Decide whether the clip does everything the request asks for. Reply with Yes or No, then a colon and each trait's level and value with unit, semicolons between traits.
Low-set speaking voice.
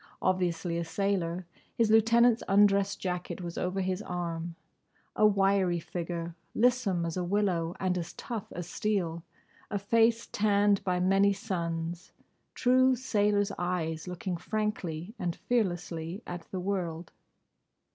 No: medium, 185 Hz